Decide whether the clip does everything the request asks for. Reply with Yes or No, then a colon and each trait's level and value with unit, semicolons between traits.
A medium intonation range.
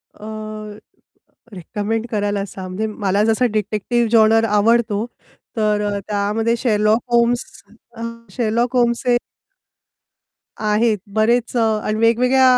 No: narrow, 2.1 semitones